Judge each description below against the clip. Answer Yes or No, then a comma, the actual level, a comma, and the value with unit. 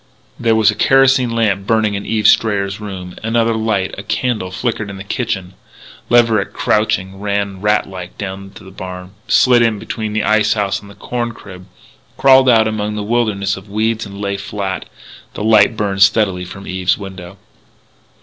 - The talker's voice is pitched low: Yes, low, 105 Hz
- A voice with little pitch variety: Yes, narrow, 2.3 semitones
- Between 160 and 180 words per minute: Yes, average, 175 wpm